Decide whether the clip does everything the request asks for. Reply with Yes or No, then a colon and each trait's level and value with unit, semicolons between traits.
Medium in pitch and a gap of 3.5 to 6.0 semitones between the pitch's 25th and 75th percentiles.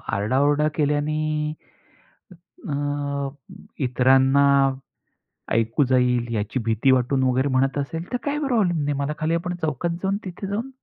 Yes: medium, 145 Hz; average, 4.0 semitones